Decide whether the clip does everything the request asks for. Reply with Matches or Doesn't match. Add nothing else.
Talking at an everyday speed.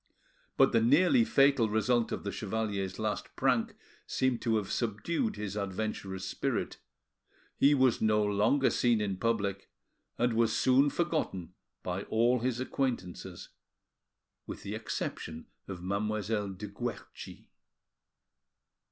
Doesn't match